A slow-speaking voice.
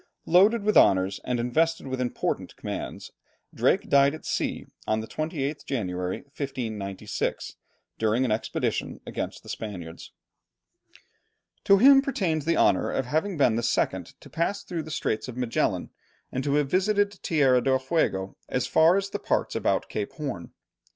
No: average, 155 wpm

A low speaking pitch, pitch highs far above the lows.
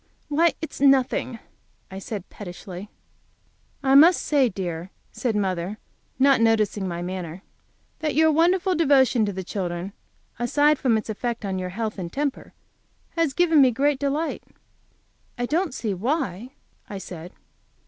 No: high, 235 Hz; wide, 7.2 semitones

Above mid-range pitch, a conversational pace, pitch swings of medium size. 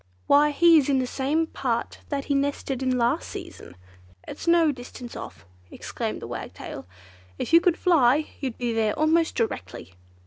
Yes: very high, 275 Hz; average, 170 wpm; average, 4.5 semitones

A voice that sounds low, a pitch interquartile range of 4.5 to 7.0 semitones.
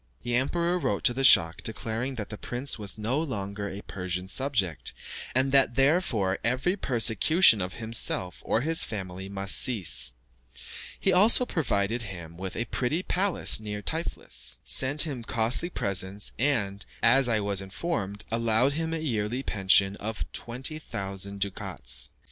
Yes: low, 115 Hz; wide, 5.5 semitones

